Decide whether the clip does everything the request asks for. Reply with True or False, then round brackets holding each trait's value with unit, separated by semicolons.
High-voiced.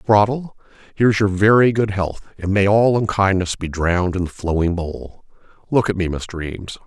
False (100 Hz)